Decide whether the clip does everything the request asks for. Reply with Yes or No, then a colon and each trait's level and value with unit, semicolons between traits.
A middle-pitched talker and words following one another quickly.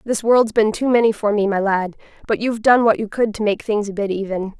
No: high, 215 Hz; fast, 275 wpm